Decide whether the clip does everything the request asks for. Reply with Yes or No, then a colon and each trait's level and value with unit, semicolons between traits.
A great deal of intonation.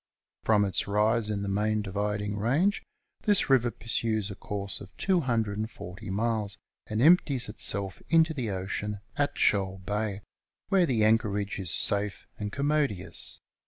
No: average, 2.9 semitones